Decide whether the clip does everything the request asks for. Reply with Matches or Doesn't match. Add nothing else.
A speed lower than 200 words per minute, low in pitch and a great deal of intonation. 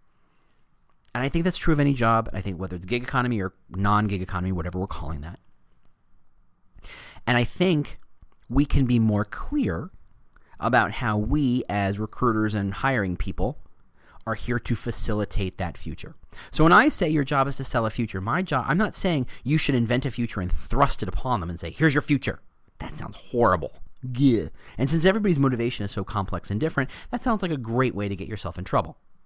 Doesn't match